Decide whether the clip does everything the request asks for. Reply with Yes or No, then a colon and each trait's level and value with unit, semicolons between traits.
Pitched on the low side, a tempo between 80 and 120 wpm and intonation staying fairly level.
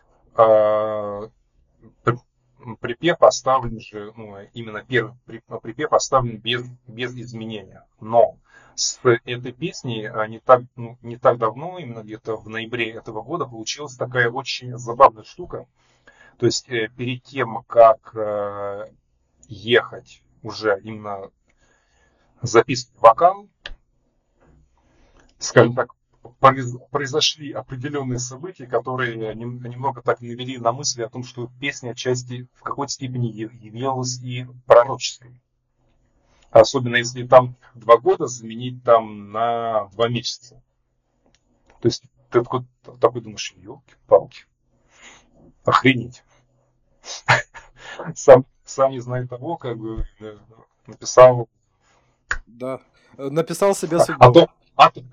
Yes: low, 120 Hz; slow, 110 wpm; narrow, 2.3 semitones